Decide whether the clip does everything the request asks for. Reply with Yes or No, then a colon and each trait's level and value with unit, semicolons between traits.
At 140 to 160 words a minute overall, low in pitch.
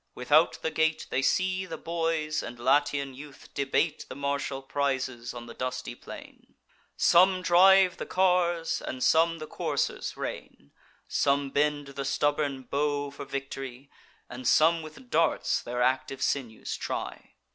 No: average, 145 wpm; medium, 145 Hz